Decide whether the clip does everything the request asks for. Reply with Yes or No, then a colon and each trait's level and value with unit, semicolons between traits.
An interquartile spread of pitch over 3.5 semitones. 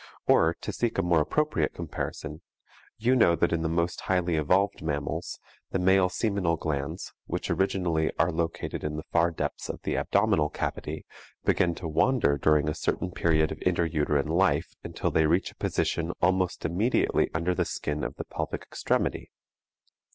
No: average, 2.8 semitones